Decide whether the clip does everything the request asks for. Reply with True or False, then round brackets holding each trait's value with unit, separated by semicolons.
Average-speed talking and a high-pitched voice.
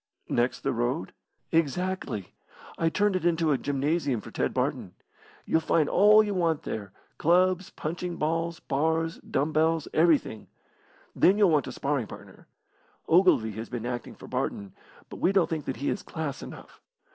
False (165 wpm; 160 Hz)